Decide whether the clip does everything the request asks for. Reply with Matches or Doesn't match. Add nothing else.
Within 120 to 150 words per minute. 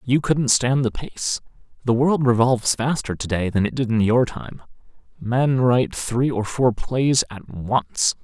Doesn't match